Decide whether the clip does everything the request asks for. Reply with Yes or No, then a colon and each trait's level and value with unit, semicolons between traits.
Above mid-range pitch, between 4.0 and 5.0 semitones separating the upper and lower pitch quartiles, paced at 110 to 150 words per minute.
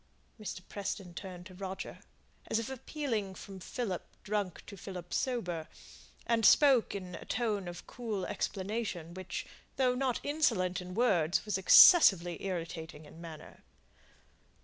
Yes: high, 195 Hz; average, 4.4 semitones; slow, 135 wpm